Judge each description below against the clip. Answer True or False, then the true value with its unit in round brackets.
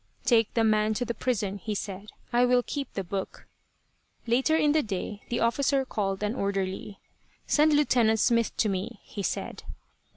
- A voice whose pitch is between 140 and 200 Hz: False (220 Hz)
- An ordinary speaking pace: True (170 wpm)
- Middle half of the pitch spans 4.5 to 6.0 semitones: False (3.7 semitones)